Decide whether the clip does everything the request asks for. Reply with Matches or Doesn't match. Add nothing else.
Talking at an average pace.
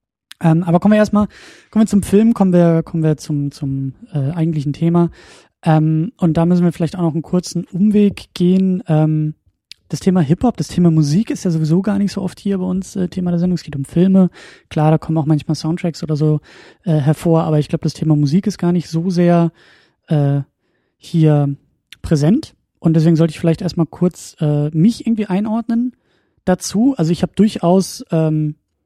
Doesn't match